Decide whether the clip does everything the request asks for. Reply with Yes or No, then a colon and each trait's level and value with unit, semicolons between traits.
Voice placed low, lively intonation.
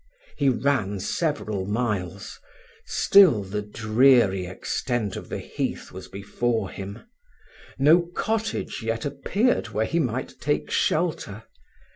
Yes: low, 115 Hz; wide, 6.0 semitones